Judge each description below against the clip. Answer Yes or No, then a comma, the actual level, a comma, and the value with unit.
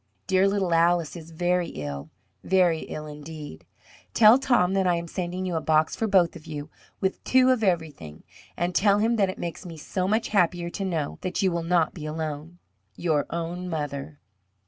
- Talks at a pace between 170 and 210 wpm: Yes, average, 190 wpm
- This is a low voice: No, medium, 175 Hz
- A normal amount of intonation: Yes, average, 3.2 semitones